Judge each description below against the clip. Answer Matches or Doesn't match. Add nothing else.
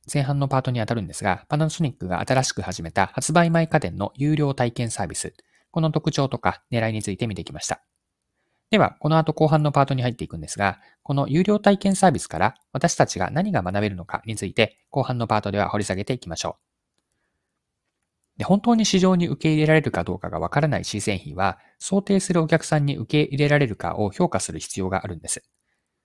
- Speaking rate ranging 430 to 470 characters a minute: Matches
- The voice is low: Matches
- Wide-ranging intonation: Matches